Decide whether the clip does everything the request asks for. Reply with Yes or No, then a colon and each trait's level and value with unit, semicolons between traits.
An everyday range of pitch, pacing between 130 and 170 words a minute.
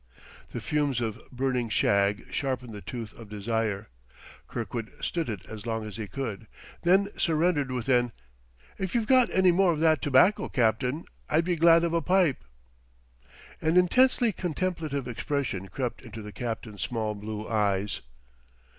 No: wide, 7.2 semitones; average, 155 wpm